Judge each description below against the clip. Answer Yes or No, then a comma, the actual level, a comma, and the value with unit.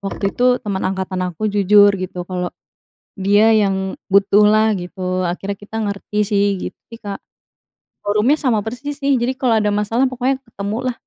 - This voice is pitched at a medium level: No, high, 205 Hz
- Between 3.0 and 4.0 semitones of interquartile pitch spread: No, narrow, 2.6 semitones